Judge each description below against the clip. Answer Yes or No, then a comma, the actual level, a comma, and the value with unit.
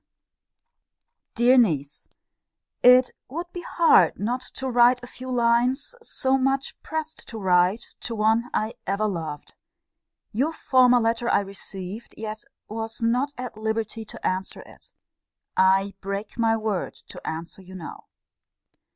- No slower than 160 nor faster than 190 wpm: No, average, 140 wpm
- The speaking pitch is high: Yes, high, 225 Hz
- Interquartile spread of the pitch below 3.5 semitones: No, average, 4.2 semitones